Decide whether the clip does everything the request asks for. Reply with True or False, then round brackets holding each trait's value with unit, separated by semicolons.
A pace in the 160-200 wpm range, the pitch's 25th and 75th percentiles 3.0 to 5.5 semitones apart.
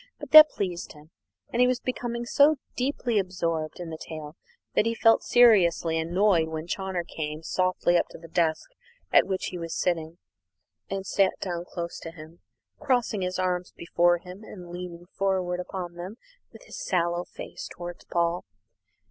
False (170 wpm; 2.6 semitones)